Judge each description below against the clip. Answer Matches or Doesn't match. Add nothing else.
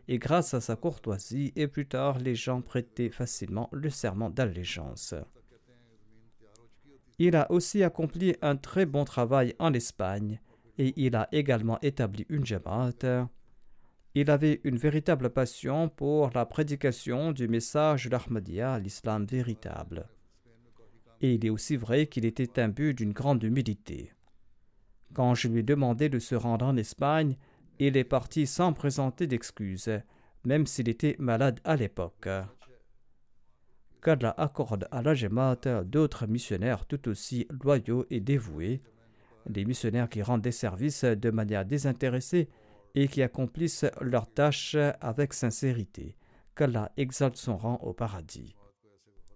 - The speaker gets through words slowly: Matches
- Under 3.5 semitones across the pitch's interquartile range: Doesn't match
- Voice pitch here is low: Matches